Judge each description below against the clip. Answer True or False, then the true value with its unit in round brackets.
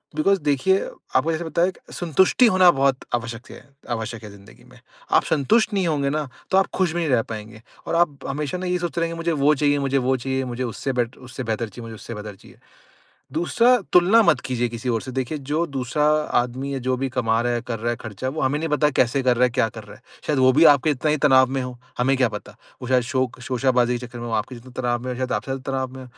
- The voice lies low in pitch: True (130 Hz)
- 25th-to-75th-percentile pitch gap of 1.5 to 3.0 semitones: False (4.0 semitones)